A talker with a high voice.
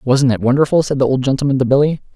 No: low, 135 Hz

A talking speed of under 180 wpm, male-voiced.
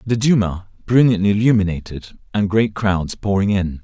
Yes: average, 140 wpm; male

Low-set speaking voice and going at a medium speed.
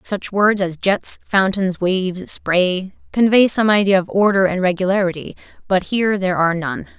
No: high, 190 Hz; average, 165 wpm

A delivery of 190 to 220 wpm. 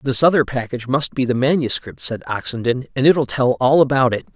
Yes: fast, 205 wpm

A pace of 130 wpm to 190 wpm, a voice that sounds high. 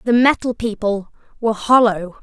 Yes: slow, 135 wpm; high, 220 Hz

